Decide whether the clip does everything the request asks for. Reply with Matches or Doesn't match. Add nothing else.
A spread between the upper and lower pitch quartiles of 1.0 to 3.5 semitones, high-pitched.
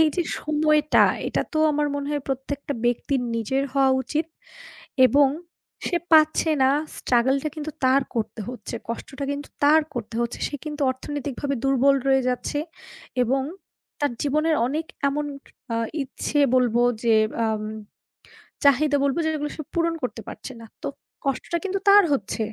Matches